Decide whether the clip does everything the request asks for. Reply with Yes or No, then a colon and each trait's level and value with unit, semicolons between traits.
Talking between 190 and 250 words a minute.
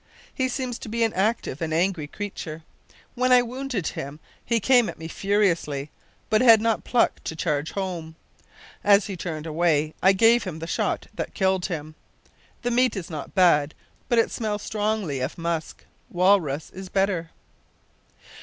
No: average, 170 wpm